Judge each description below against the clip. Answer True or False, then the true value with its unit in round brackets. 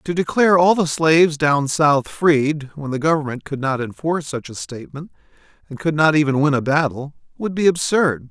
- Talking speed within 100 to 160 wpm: False (195 wpm)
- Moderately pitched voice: True (150 Hz)